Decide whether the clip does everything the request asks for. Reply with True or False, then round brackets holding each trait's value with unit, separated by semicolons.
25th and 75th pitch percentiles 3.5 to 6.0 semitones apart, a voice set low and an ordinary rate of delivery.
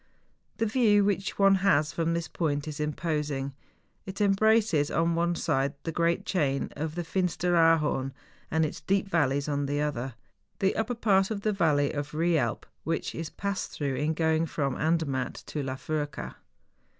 False (4.7 semitones; 160 Hz; 165 wpm)